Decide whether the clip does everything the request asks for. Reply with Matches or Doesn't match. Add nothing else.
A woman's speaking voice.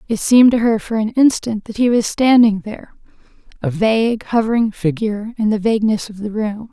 Matches